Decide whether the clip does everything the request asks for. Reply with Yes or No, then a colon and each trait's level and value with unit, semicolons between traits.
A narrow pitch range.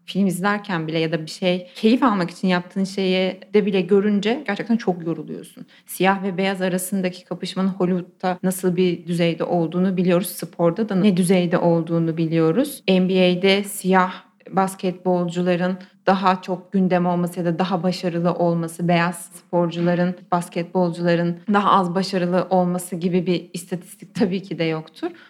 Yes: narrow, 1.6 semitones